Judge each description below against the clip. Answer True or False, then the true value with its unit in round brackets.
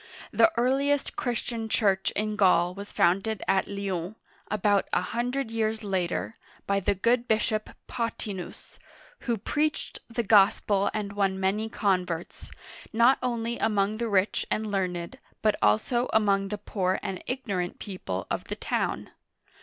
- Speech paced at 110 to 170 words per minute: True (140 wpm)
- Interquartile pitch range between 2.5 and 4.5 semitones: True (3.1 semitones)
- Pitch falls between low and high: False (210 Hz)